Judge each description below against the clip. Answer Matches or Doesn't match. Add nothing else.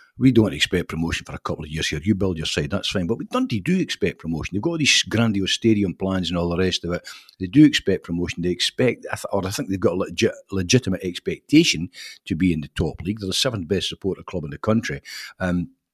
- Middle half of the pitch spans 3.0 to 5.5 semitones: Matches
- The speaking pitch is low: Matches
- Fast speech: Matches